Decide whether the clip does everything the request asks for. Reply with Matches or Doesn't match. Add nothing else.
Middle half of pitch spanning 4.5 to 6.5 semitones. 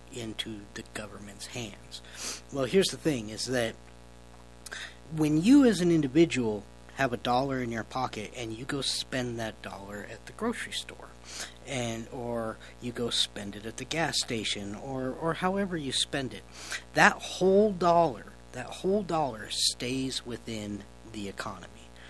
Matches